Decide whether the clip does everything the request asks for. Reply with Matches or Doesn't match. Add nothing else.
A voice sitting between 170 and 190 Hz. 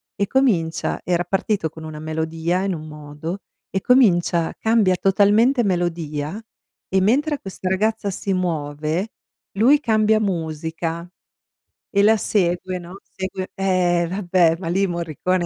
Matches